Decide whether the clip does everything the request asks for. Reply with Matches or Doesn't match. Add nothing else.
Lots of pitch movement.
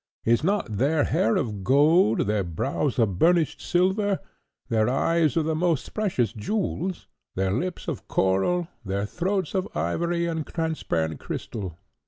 Matches